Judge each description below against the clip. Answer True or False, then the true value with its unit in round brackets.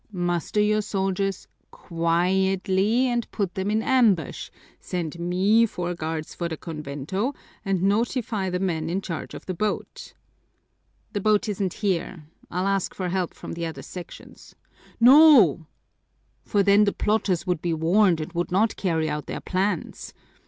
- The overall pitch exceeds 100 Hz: True (190 Hz)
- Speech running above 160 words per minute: False (150 wpm)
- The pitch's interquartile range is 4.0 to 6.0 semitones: False (3.5 semitones)